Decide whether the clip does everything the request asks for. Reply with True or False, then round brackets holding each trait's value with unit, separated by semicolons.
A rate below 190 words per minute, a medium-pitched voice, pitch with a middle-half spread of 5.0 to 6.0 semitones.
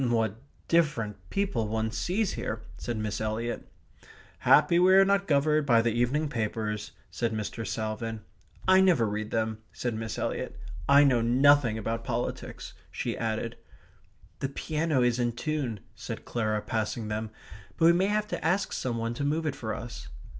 False (170 wpm; 120 Hz; 5.4 semitones)